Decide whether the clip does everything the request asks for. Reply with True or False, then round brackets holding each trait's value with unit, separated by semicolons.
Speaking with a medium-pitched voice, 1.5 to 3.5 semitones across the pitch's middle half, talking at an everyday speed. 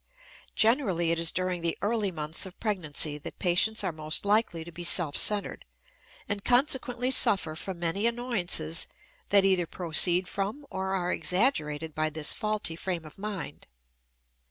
False (180 Hz; 4.3 semitones; 155 wpm)